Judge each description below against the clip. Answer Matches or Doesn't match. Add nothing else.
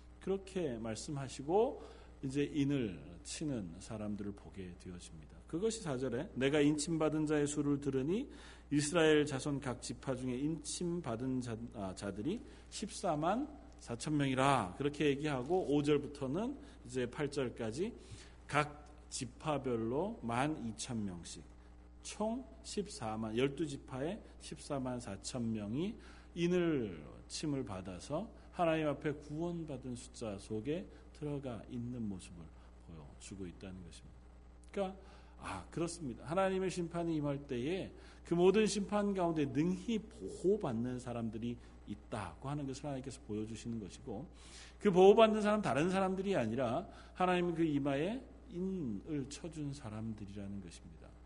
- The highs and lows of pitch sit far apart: Matches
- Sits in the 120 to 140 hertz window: Matches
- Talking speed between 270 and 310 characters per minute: Matches